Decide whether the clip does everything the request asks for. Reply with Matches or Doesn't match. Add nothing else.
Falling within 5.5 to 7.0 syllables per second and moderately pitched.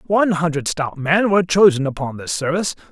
Matches